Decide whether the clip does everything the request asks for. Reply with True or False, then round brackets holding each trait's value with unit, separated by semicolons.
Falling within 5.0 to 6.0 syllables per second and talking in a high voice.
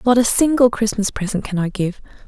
True (5.7 syllables/s; 220 Hz)